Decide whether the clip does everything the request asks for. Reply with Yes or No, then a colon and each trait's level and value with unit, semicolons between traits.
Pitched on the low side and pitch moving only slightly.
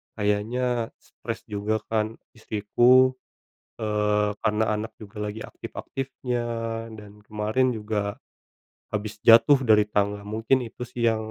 Yes: low, 110 Hz; narrow, 2.2 semitones